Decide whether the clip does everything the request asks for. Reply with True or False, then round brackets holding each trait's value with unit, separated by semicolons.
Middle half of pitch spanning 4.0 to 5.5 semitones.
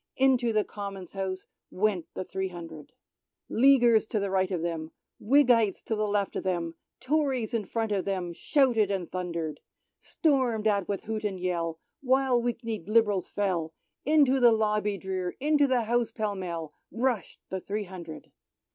True (4.5 semitones)